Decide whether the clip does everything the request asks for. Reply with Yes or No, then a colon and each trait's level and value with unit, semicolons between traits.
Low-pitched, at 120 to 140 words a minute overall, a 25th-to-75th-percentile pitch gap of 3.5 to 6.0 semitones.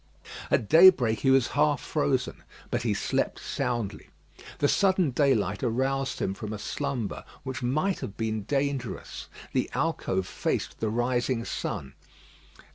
Yes: low, 125 Hz; slow, 135 wpm; average, 4.4 semitones